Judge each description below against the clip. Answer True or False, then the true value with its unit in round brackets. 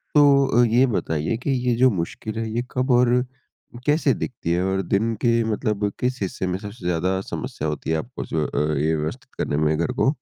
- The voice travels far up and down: True (6.6 semitones)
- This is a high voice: False (110 Hz)